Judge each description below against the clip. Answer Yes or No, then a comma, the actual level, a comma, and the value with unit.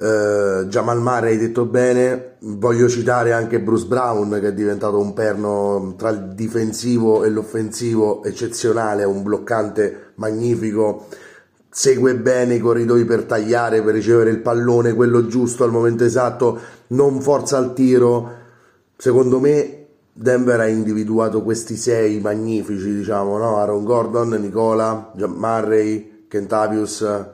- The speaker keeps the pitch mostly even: Yes, narrow, 2.0 semitones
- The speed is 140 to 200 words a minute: No, average, 130 wpm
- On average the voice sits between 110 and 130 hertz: Yes, low, 115 Hz